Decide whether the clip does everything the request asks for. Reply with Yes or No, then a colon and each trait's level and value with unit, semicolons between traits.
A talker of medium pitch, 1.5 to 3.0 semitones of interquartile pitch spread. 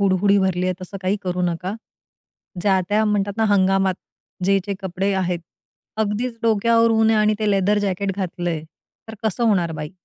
No: high, 195 Hz; narrow, 2.4 semitones